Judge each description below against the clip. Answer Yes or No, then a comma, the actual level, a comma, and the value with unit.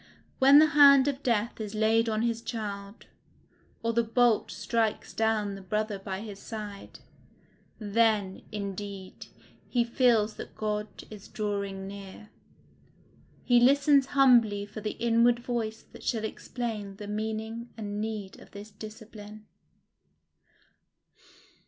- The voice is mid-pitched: No, high, 220 Hz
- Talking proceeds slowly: Yes, slow, 125 wpm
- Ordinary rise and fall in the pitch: No, narrow, 2.3 semitones